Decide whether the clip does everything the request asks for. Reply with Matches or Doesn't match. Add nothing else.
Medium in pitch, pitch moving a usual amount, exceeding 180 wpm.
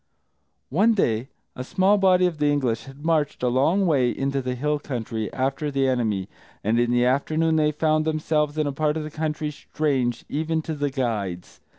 Matches